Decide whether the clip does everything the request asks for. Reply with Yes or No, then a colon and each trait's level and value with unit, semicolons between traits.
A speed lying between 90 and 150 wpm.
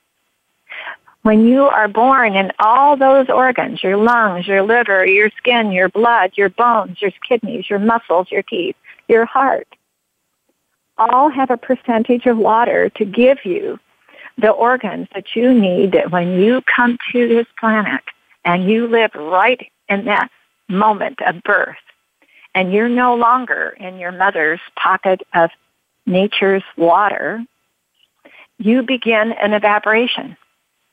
Yes: average, 140 wpm